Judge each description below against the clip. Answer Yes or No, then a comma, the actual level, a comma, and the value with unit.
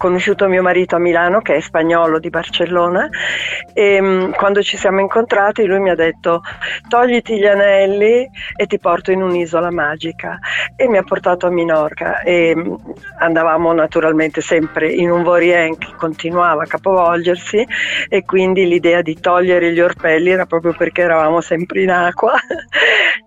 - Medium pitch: Yes, medium, 175 Hz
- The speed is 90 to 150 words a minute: No, average, 160 wpm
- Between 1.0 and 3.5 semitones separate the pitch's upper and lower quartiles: Yes, narrow, 2.5 semitones